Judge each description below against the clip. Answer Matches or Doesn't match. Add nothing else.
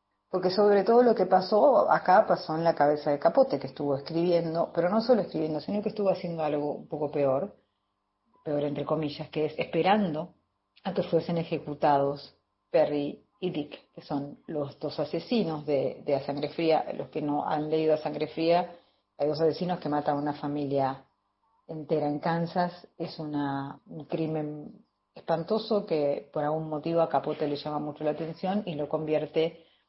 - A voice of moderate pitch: Matches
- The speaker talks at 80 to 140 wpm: Doesn't match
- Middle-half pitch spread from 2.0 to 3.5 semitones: Matches